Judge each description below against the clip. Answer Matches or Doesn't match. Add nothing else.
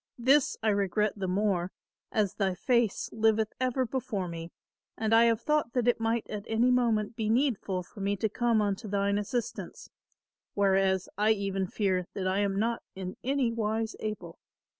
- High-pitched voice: Matches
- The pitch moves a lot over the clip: Doesn't match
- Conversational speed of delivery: Matches